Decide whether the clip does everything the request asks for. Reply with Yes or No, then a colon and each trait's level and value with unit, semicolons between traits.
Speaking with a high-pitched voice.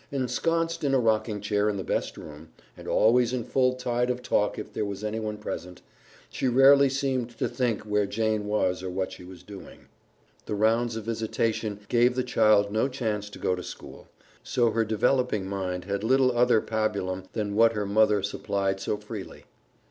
No: low, 110 Hz